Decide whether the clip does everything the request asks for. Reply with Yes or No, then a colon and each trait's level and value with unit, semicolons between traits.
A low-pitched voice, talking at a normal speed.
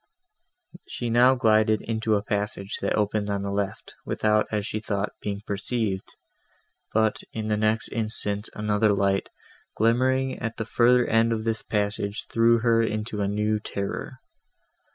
Yes: low, 110 Hz; average, 150 wpm